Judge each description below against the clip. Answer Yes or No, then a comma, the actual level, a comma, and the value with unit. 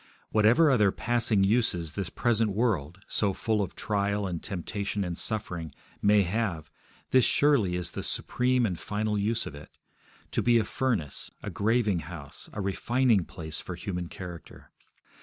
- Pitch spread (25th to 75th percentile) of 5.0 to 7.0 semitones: No, average, 4.4 semitones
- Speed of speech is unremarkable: Yes, average, 160 wpm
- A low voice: Yes, low, 100 Hz